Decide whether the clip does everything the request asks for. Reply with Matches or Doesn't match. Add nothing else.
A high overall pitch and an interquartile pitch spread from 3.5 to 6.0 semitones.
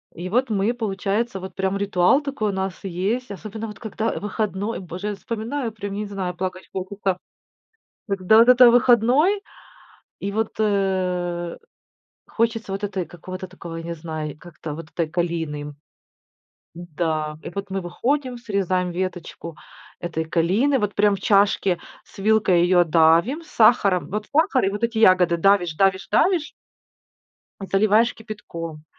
Matches